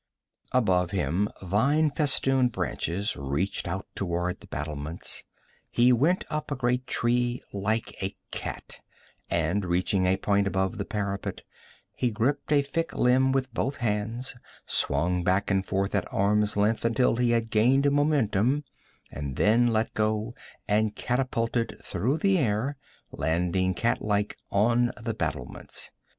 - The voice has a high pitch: No, low, 110 Hz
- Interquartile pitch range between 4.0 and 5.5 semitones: Yes, average, 4.6 semitones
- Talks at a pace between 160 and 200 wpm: No, average, 140 wpm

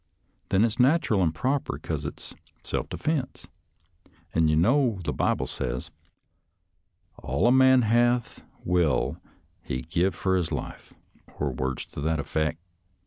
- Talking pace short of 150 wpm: Yes, average, 140 wpm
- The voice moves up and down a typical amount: No, wide, 7.5 semitones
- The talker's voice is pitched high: No, very low, 95 Hz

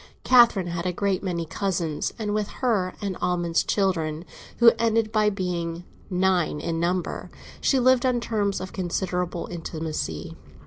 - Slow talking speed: No, average, 145 wpm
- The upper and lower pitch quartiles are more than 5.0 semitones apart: No, average, 3.6 semitones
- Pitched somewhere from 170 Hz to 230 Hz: Yes, medium, 185 Hz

